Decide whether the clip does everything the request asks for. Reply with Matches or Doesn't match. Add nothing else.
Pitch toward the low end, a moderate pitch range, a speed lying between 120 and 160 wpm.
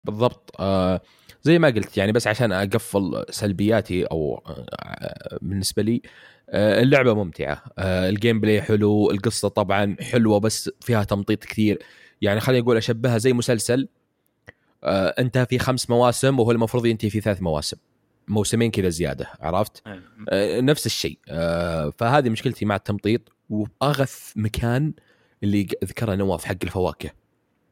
Matches